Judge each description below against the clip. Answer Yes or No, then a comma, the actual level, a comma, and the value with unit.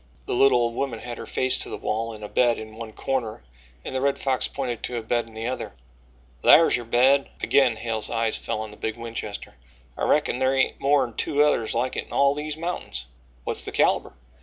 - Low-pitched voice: Yes, low, 120 Hz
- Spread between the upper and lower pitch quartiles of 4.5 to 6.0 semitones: No, average, 3.2 semitones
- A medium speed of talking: No, fast, 225 wpm